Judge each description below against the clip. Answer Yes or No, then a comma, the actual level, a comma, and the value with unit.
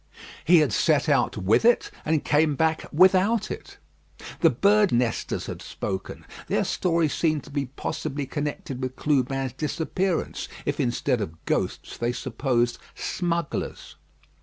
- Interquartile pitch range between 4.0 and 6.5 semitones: Yes, average, 4.4 semitones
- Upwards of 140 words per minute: No, slow, 135 wpm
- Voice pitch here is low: No, medium, 145 Hz